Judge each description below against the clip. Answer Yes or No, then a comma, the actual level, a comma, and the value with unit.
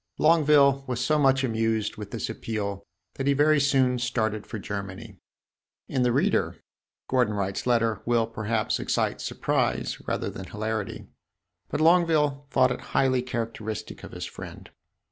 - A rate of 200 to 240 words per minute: No, average, 145 wpm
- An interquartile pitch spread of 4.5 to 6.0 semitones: No, average, 4.0 semitones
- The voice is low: Yes, low, 120 Hz